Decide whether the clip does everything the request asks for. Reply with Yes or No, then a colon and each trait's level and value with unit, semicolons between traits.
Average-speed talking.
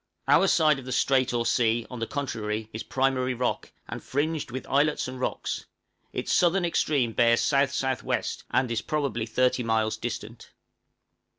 Yes: average, 160 wpm